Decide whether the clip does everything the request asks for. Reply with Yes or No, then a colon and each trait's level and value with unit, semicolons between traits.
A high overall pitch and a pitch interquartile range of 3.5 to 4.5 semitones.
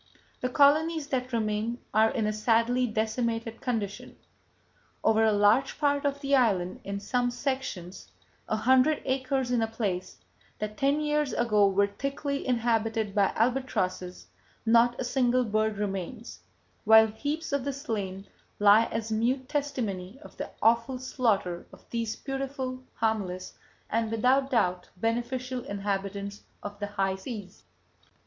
Yes: high, 230 Hz; average, 3.9 semitones